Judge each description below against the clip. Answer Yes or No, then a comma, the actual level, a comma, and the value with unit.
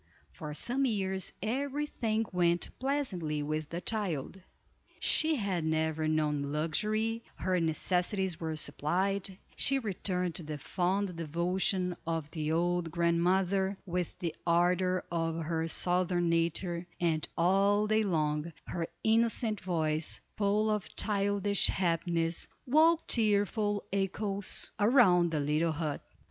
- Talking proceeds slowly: Yes, slow, 120 wpm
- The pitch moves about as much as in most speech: Yes, average, 3.7 semitones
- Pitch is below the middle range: No, medium, 180 Hz